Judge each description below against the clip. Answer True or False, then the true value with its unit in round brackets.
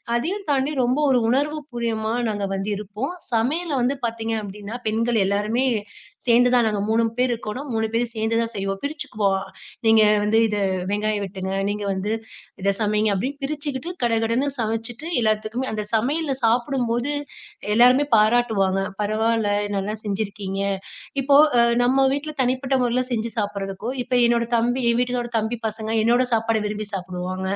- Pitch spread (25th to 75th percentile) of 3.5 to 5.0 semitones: False (3.0 semitones)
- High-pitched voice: True (225 Hz)